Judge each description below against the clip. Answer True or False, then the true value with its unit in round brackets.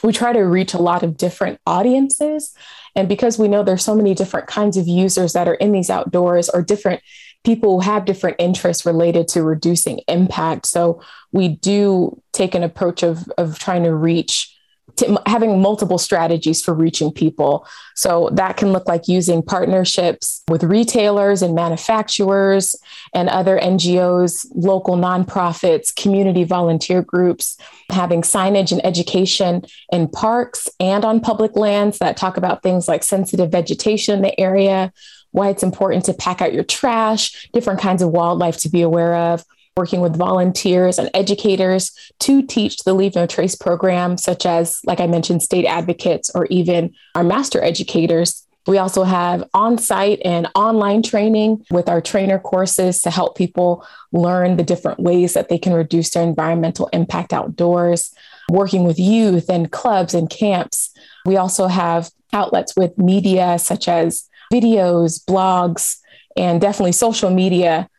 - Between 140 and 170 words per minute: True (160 wpm)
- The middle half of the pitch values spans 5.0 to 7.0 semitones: False (2.6 semitones)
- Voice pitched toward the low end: False (185 Hz)